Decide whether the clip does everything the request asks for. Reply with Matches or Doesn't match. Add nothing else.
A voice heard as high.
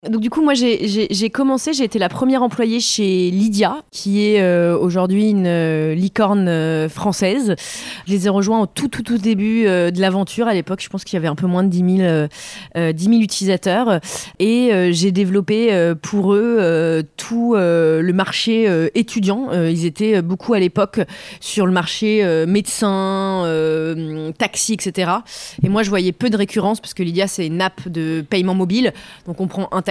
Matches